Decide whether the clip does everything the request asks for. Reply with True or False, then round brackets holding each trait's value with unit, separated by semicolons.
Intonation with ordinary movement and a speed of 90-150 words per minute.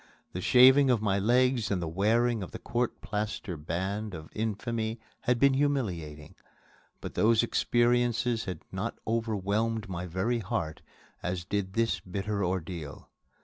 True (4.2 semitones; 145 wpm)